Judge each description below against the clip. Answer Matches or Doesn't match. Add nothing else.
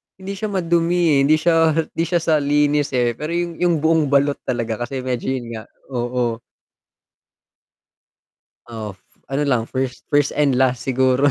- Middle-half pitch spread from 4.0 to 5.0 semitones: Matches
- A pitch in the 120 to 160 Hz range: Matches